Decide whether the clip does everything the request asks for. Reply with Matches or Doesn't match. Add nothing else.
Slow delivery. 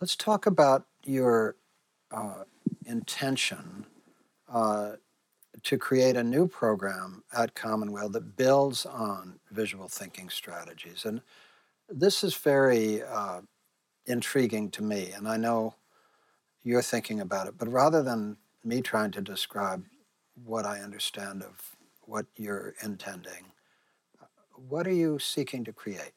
Matches